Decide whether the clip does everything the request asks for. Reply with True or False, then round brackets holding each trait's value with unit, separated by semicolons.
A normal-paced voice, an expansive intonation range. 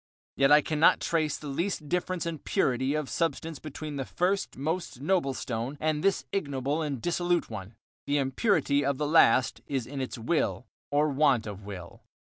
False (175 wpm; 3.7 semitones)